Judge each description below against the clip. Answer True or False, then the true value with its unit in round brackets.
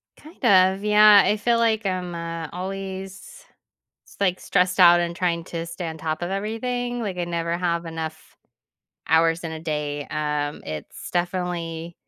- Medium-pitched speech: True (175 Hz)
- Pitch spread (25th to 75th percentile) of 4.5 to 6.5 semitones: False (2.9 semitones)